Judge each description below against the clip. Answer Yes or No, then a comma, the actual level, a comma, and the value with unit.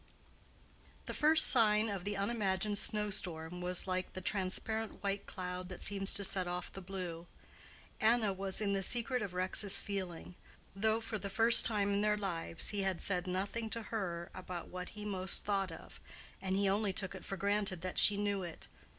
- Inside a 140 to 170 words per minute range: No, average, 190 wpm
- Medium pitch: No, high, 195 Hz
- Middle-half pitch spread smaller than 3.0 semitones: Yes, narrow, 2.4 semitones